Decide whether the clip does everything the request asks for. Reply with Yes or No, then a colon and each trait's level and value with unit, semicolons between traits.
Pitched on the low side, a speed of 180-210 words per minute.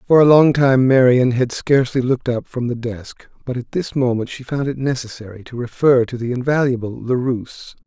Yes: low, 125 Hz; average, 200 wpm